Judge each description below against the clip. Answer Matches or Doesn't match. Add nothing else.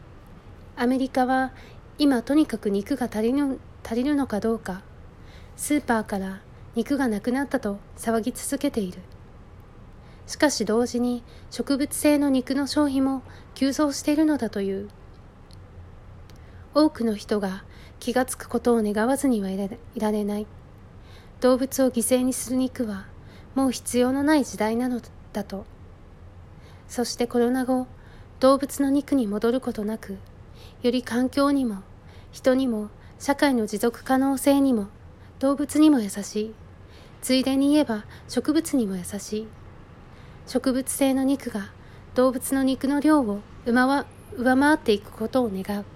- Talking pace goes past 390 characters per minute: Doesn't match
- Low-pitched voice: Doesn't match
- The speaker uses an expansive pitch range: Doesn't match